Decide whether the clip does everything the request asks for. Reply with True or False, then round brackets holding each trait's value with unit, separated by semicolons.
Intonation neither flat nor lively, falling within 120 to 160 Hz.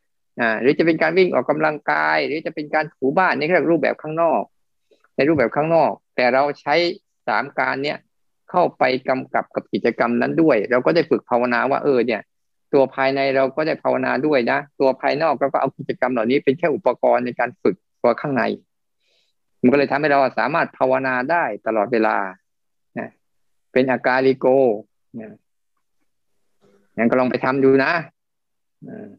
True (3.4 semitones; 130 Hz)